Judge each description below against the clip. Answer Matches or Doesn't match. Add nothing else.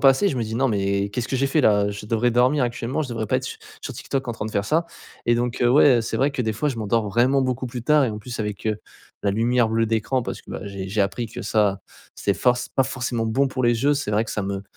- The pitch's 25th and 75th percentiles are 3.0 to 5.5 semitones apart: Matches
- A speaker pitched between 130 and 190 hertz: Doesn't match